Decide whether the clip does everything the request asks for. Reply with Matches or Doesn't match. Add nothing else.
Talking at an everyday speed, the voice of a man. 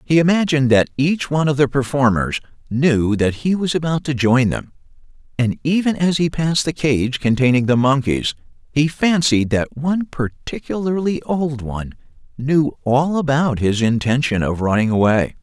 Matches